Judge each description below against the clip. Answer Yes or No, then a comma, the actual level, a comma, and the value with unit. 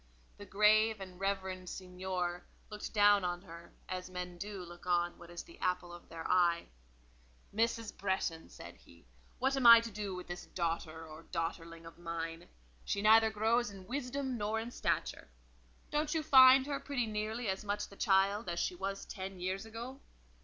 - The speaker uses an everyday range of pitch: Yes, average, 4.0 semitones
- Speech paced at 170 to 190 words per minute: Yes, average, 180 wpm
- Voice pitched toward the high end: Yes, high, 195 Hz